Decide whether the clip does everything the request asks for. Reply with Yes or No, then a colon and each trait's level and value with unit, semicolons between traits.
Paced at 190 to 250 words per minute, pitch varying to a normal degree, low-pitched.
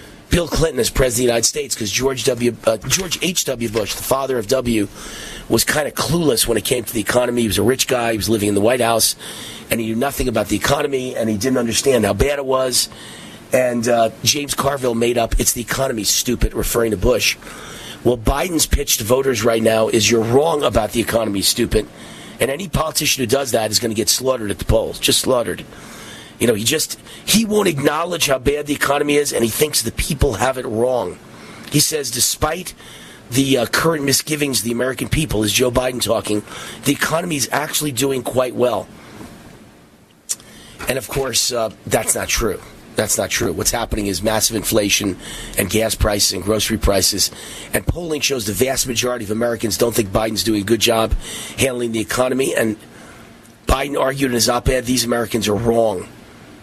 Yes: average, 200 wpm; average, 3.4 semitones; low, 120 Hz